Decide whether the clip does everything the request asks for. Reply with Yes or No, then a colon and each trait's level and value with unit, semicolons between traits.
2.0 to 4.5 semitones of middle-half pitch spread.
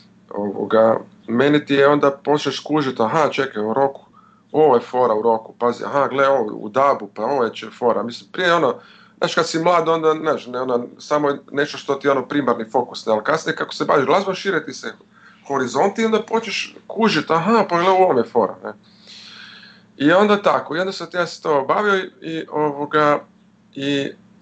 No: wide, 5.6 semitones